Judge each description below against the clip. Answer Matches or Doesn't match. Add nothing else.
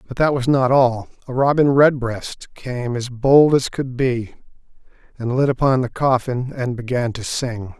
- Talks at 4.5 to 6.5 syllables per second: Doesn't match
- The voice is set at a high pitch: Doesn't match